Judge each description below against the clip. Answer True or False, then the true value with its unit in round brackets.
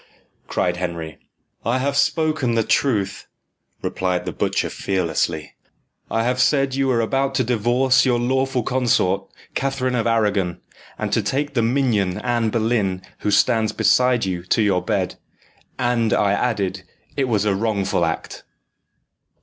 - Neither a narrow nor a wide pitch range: True (4.7 semitones)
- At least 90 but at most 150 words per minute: True (145 wpm)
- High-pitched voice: False (115 Hz)